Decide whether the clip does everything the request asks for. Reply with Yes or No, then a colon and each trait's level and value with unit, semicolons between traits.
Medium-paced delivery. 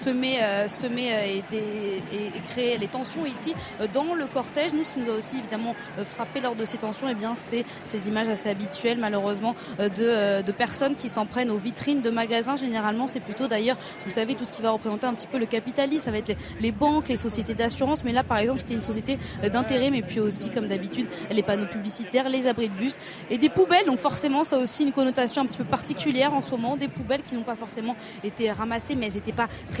No: fast, 235 wpm